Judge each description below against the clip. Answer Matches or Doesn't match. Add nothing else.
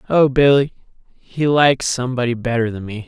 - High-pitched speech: Doesn't match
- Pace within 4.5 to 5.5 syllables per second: Doesn't match